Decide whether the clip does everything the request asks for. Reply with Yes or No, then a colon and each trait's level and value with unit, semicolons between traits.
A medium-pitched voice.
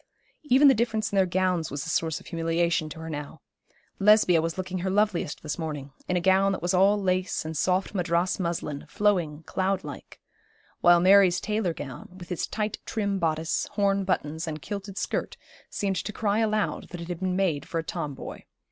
Yes: medium, 180 Hz